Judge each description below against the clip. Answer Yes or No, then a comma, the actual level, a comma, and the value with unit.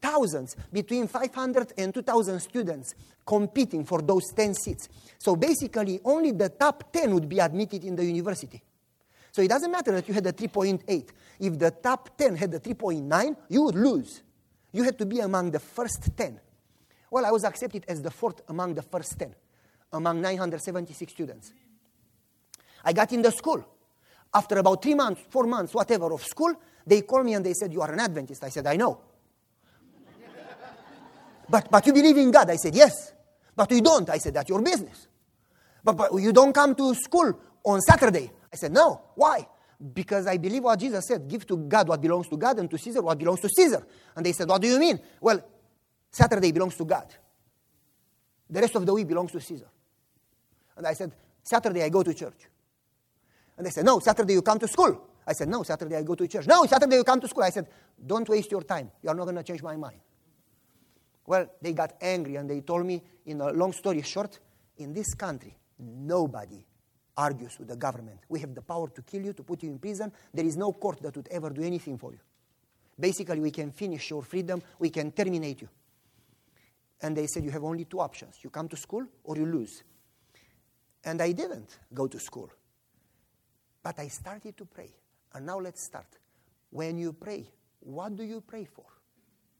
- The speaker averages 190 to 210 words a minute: Yes, average, 200 wpm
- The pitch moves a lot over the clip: Yes, wide, 6.2 semitones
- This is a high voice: No, medium, 180 Hz